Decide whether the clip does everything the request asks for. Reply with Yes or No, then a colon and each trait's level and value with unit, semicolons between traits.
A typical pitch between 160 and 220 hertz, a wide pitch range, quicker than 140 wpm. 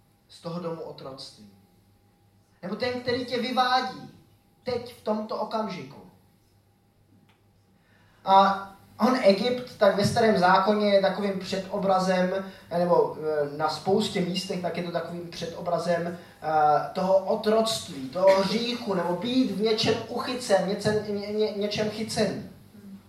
No: high, 190 Hz; wide, 6.3 semitones; average, 120 wpm